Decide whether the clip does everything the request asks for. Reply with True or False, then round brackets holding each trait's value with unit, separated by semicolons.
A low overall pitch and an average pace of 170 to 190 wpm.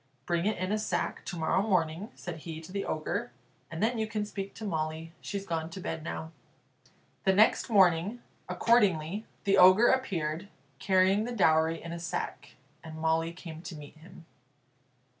False (180 Hz; 175 wpm)